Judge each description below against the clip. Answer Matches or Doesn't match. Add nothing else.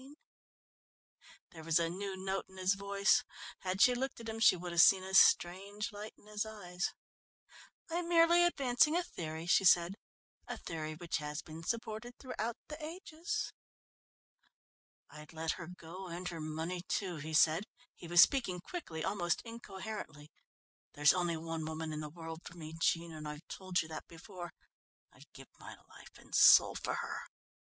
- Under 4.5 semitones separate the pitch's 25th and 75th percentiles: Doesn't match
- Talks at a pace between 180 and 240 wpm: Doesn't match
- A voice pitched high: Doesn't match